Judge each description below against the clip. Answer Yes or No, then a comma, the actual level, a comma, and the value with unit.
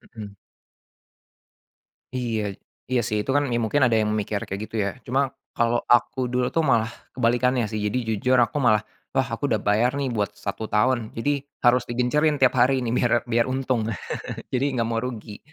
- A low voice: Yes, low, 120 Hz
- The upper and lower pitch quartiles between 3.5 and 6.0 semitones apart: No, average, 2.8 semitones